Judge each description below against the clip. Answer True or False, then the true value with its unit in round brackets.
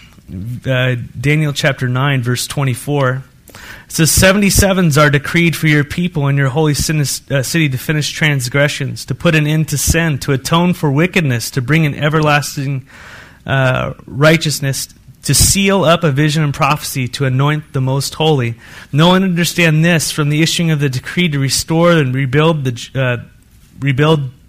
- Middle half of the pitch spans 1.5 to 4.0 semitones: True (3.3 semitones)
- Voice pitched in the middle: True (145 Hz)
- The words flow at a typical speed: True (160 wpm)